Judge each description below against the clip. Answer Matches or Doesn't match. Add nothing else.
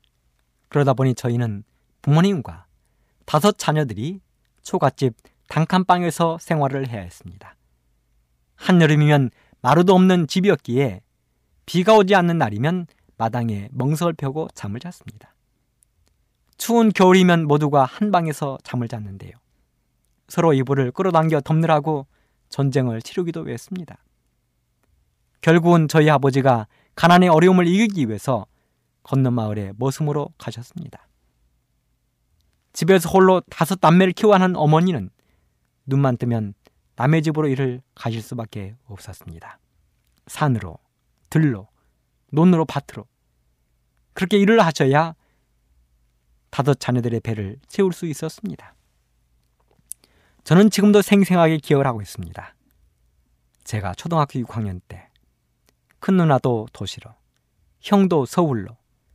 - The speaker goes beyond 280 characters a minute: Doesn't match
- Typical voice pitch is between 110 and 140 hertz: Matches